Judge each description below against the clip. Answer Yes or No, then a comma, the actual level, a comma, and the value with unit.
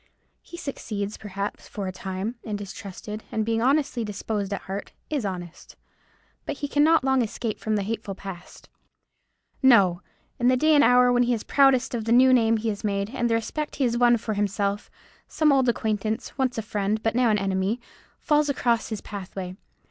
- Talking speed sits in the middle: Yes, average, 195 wpm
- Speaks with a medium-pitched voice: No, high, 225 Hz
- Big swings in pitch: No, average, 3.8 semitones